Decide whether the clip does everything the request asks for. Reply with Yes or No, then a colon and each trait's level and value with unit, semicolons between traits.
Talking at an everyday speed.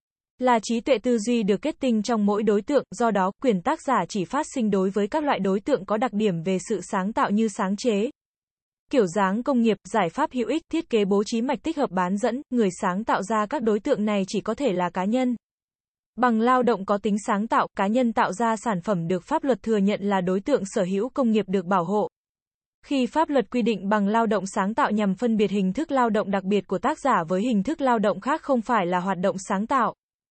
No: fast, 255 wpm